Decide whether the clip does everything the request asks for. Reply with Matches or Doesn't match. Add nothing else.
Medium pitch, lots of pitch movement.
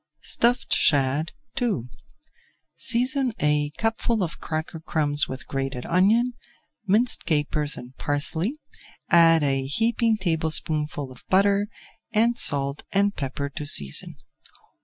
Matches